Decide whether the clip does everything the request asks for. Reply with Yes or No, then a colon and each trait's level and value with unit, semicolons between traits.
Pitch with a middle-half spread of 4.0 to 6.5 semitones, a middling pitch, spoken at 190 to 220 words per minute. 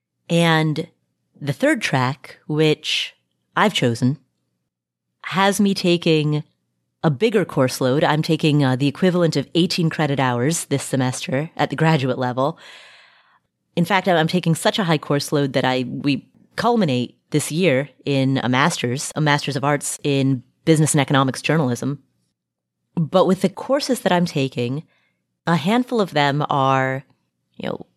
No: average, 4.7 semitones; medium, 145 Hz; average, 150 wpm